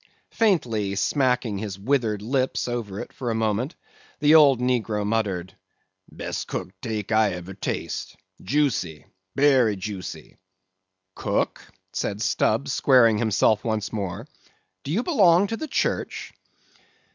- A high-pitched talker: No, low, 110 Hz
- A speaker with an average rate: No, slow, 125 wpm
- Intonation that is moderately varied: Yes, average, 4.9 semitones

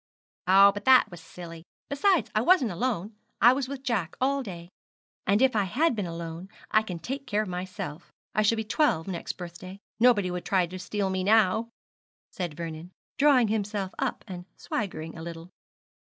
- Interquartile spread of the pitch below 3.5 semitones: No, average, 4.8 semitones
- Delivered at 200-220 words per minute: No, average, 180 wpm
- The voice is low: No, high, 195 Hz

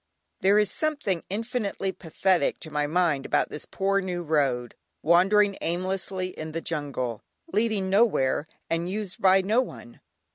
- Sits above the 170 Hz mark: Yes, medium, 185 Hz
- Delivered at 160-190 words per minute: No, average, 145 wpm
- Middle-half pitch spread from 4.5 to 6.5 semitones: No, average, 4.1 semitones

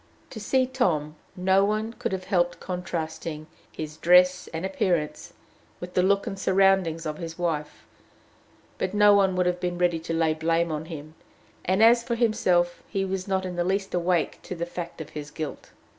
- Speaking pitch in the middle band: Yes, medium, 180 Hz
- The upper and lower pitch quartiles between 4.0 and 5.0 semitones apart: No, average, 2.8 semitones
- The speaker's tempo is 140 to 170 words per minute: No, average, 190 wpm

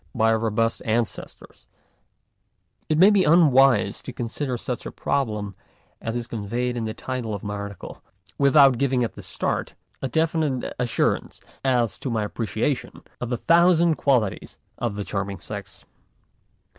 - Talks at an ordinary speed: Yes, average, 155 wpm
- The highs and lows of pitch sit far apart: No, average, 4.0 semitones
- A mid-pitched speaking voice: No, low, 120 Hz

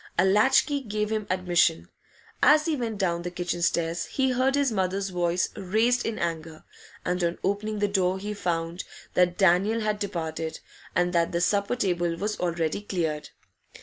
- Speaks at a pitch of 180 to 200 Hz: Yes, medium, 185 Hz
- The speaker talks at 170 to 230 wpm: Yes, average, 175 wpm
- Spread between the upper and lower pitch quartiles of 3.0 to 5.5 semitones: Yes, average, 3.7 semitones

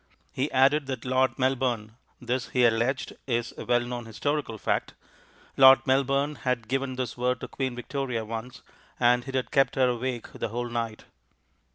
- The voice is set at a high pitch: No, low, 125 Hz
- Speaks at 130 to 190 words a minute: Yes, average, 170 wpm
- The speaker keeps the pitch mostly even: Yes, narrow, 1.9 semitones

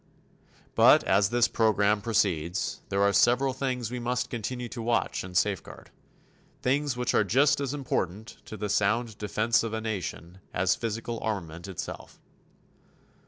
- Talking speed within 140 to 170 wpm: Yes, average, 150 wpm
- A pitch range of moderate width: Yes, average, 3.5 semitones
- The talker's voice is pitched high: No, low, 110 Hz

